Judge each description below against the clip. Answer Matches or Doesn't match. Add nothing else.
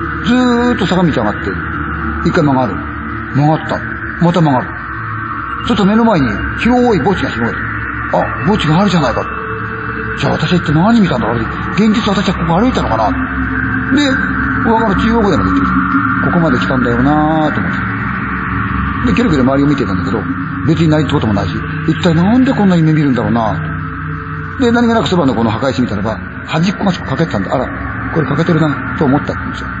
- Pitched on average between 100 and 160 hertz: Matches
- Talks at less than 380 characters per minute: Doesn't match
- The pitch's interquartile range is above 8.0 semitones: Matches